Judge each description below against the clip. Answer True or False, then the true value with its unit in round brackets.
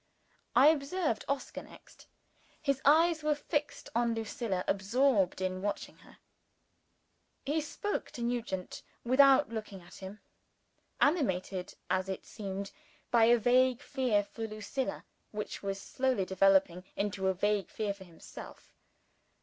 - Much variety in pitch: True (5.7 semitones)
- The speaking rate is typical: False (130 wpm)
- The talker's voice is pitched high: True (225 Hz)